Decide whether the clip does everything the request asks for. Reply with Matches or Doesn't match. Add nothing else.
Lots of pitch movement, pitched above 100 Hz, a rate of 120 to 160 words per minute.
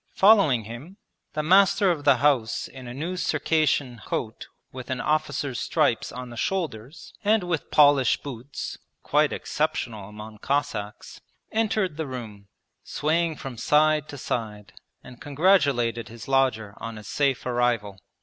Doesn't match